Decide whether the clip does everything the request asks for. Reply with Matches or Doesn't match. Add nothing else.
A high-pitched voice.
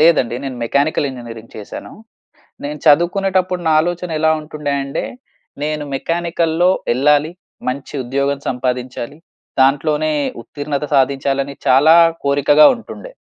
Doesn't match